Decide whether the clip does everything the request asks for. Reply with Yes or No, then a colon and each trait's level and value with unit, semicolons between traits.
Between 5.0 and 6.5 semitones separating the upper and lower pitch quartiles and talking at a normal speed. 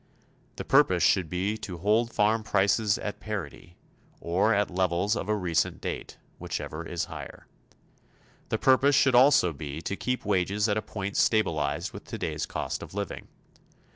No: average, 3.8 semitones; average, 160 wpm